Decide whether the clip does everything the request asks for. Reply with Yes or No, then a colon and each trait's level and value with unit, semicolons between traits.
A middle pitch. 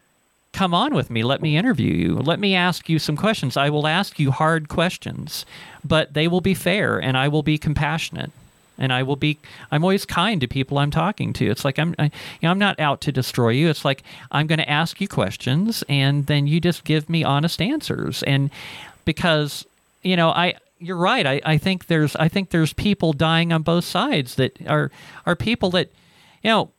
Yes: medium, 155 Hz